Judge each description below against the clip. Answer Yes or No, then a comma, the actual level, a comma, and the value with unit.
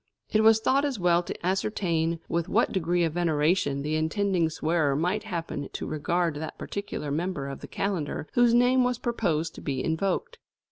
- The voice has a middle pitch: Yes, medium, 175 Hz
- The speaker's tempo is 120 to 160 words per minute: No, average, 180 wpm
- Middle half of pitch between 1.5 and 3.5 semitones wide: No, average, 4.6 semitones